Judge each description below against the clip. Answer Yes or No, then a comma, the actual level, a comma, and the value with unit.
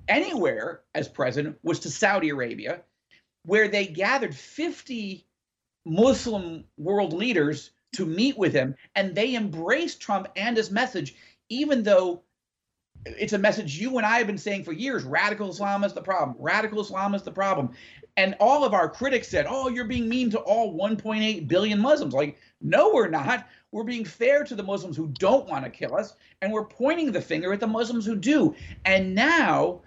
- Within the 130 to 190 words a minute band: Yes, average, 185 wpm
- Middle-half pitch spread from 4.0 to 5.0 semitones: Yes, average, 4.3 semitones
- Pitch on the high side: Yes, high, 210 Hz